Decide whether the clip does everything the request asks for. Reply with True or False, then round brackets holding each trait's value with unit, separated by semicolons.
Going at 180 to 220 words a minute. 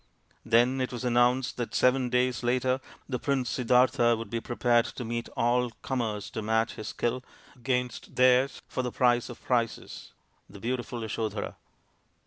False (155 wpm)